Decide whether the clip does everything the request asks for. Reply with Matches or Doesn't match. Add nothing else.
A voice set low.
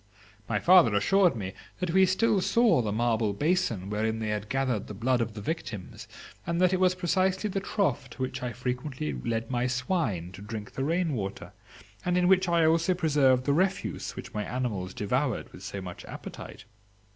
Matches